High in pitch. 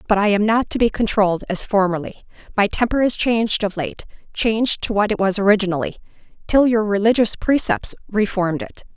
Yes: high, 210 Hz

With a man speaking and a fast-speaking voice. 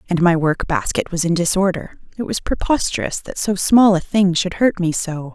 No: female; fast, 215 wpm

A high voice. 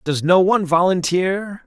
No: medium, 180 Hz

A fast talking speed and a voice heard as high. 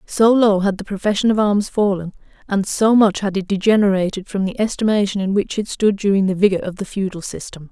Yes: fast, 220 wpm; high, 200 Hz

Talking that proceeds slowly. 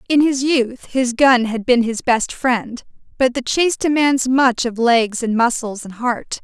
No: average, 195 wpm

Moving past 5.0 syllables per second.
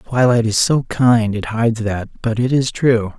No: 4.8 syllables/s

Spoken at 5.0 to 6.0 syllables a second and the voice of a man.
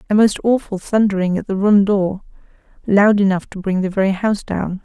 No: 5.5 syllables/s; female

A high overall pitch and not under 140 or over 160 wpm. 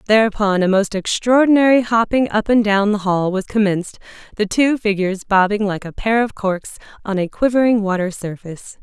No: high, 210 Hz; average, 175 wpm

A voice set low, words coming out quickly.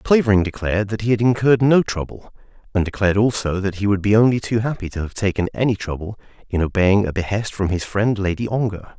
Yes: low, 105 Hz; fast, 215 wpm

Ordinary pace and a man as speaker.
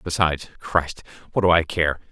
Yes: average, 170 wpm; male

